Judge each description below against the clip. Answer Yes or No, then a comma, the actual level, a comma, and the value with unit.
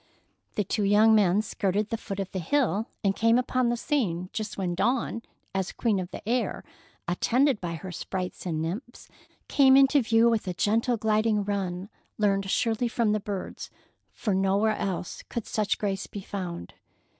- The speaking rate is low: No, average, 175 wpm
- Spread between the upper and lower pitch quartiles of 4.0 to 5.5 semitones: No, average, 3.2 semitones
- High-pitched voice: Yes, high, 210 Hz